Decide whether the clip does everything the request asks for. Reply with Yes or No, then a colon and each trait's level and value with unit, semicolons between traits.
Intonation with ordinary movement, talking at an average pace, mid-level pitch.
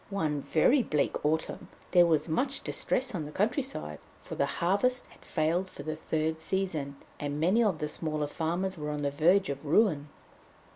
Yes: average, 4.4 semitones; average, 180 wpm; medium, 160 Hz